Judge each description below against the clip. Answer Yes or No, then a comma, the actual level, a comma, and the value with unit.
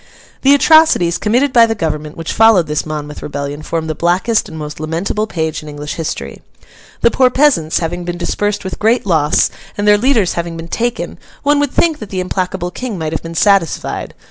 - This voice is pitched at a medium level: Yes, medium, 180 Hz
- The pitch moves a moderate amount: No, wide, 6.0 semitones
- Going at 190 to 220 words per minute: Yes, average, 195 wpm